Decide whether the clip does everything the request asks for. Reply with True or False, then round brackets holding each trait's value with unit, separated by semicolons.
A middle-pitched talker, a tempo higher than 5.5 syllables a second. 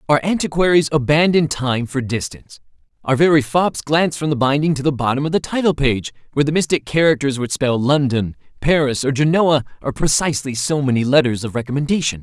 True (145 Hz; 6.0 syllables/s)